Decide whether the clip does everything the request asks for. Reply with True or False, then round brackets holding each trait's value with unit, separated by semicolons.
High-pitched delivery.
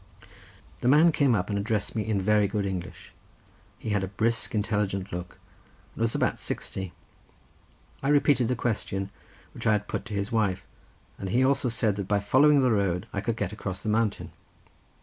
False (105 Hz)